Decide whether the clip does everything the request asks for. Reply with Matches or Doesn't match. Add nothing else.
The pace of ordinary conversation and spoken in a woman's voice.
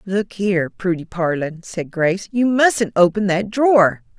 Matches